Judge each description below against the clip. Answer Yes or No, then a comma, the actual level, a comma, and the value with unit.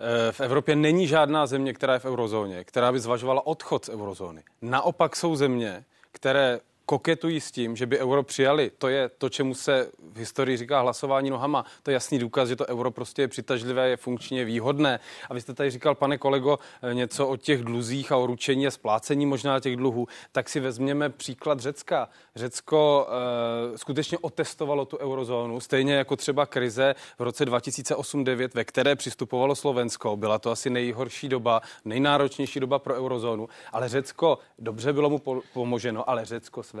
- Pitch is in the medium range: No, low, 130 Hz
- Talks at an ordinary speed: No, fast, 180 wpm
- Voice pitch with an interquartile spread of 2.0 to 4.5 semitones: Yes, narrow, 2.6 semitones